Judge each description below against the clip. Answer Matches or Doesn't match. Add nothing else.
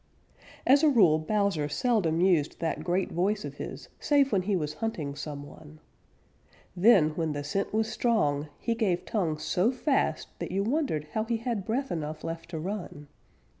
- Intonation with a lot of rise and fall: Matches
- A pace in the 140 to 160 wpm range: Doesn't match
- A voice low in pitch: Doesn't match